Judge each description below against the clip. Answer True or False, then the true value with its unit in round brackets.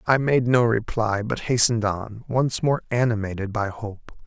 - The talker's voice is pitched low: True (115 Hz)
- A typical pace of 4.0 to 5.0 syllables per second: True (4.5 syllables/s)